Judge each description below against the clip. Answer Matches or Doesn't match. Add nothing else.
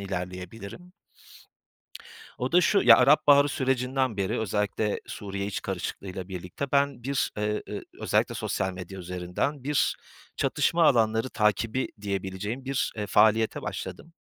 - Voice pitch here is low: Matches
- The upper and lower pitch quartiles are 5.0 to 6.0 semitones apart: Matches